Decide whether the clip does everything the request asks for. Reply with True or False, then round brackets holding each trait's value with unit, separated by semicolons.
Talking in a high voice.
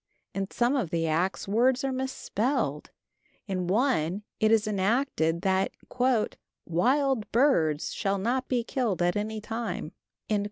True (215 Hz)